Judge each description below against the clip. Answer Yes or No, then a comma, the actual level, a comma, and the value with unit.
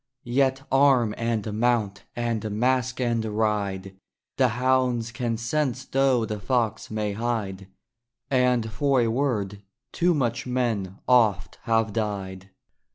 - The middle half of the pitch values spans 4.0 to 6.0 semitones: No, average, 3.1 semitones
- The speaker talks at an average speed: No, slow, 125 wpm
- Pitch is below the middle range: Yes, low, 115 Hz